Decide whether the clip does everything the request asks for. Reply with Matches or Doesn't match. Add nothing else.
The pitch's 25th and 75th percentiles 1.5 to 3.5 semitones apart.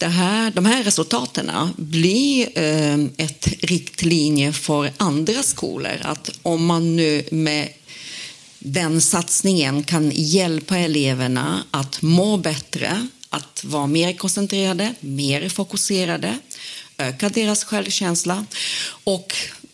Doesn't match